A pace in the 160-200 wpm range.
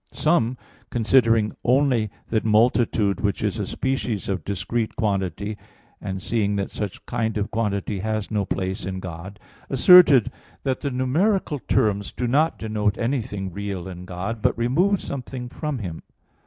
No: average, 150 wpm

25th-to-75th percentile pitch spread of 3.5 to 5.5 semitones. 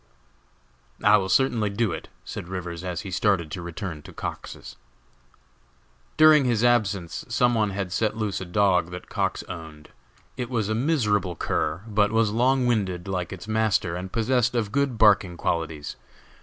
Yes: average, 4.3 semitones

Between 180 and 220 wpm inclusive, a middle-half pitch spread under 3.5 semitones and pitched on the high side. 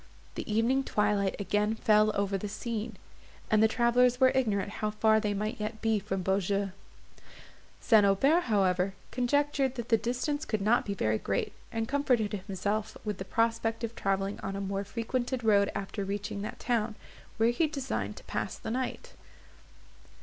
No: average, 170 wpm; average, 3.0 semitones; high, 215 Hz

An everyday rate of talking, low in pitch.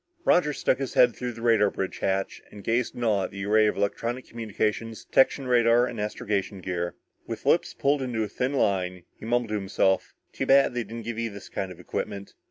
No: fast, 215 wpm; low, 110 Hz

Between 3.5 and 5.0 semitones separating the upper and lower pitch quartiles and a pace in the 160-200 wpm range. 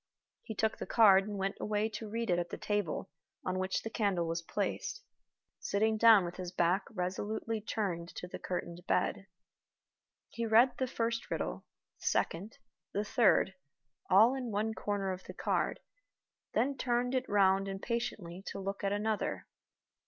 No: average, 3.1 semitones; average, 165 wpm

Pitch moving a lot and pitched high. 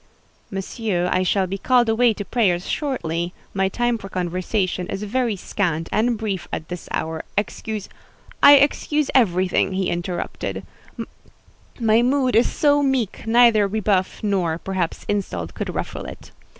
No: average, 4.5 semitones; high, 200 Hz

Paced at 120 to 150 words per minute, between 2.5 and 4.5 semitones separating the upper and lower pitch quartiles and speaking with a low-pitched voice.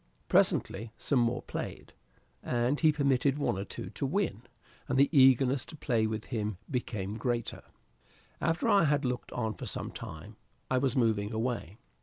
No: average, 165 wpm; average, 3.9 semitones; low, 125 Hz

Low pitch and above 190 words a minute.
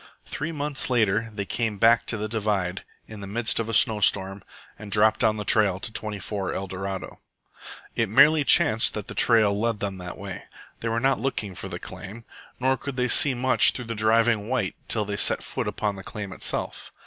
Yes: low, 110 Hz; fast, 205 wpm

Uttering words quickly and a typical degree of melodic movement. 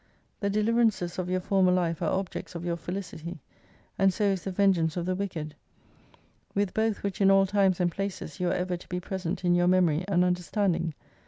No: fast, 210 wpm; narrow, 2.0 semitones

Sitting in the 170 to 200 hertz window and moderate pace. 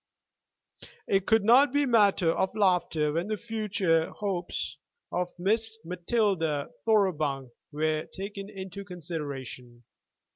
No: medium, 185 Hz; slow, 110 wpm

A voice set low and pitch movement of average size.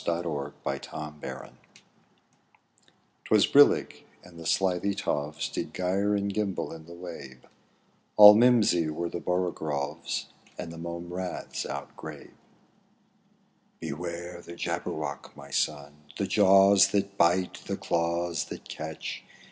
Yes: very low, 85 Hz; average, 3.4 semitones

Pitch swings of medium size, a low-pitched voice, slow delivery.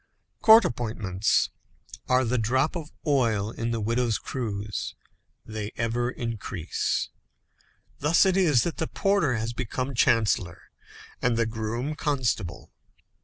Yes: average, 3.7 semitones; low, 120 Hz; slow, 120 wpm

